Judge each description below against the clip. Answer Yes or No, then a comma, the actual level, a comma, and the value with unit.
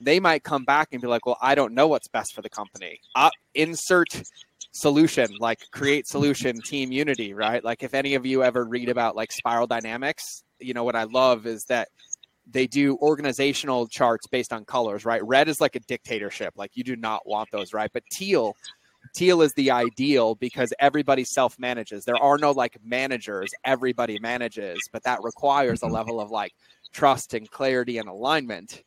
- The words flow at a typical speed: Yes, average, 190 wpm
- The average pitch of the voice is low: Yes, low, 125 Hz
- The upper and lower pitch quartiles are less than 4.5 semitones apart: Yes, average, 3.1 semitones